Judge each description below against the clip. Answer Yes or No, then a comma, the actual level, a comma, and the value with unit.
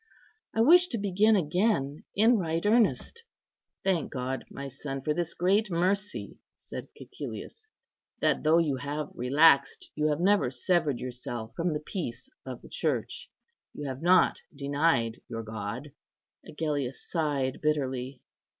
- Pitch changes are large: Yes, wide, 5.7 semitones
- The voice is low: No, medium, 150 Hz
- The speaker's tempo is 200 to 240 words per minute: No, average, 140 wpm